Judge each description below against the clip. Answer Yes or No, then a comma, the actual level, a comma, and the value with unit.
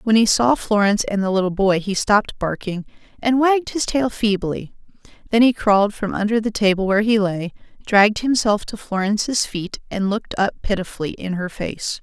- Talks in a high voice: Yes, high, 210 Hz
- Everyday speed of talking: Yes, average, 190 wpm